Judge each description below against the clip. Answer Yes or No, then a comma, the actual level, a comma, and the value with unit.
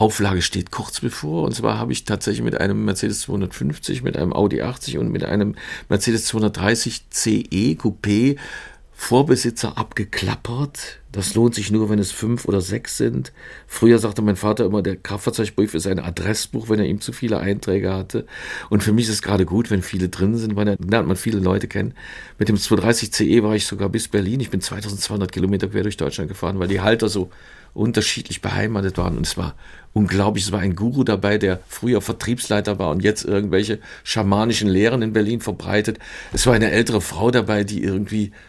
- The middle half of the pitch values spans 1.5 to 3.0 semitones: Yes, narrow, 2.4 semitones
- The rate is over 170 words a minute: Yes, fast, 190 wpm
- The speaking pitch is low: Yes, low, 105 Hz